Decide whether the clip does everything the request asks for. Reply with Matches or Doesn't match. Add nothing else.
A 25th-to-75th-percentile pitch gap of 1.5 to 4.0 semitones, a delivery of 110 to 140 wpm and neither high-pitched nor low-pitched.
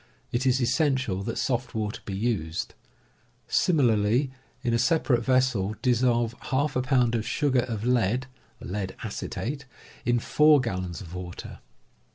Doesn't match